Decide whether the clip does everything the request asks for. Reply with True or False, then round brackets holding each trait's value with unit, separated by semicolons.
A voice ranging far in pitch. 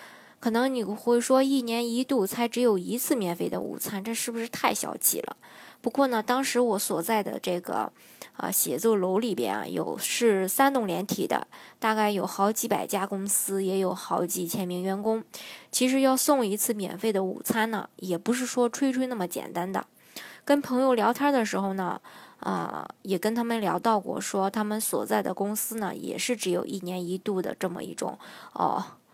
False (4.1 semitones)